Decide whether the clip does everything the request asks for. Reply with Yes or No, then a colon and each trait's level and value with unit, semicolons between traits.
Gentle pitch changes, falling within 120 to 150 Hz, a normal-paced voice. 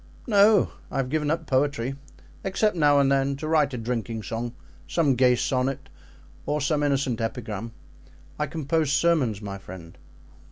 No: average, 4.3 semitones; low, 135 Hz; average, 155 wpm